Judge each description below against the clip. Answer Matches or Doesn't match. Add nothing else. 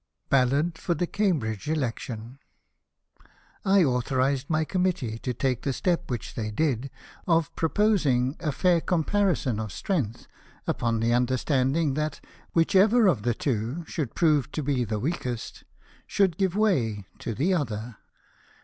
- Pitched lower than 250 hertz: Matches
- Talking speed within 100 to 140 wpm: Doesn't match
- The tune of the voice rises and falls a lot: Matches